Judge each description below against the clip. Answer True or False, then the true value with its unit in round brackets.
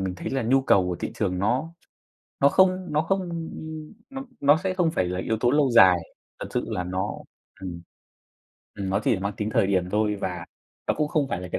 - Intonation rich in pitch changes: True (8.2 semitones)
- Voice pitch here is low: True (110 Hz)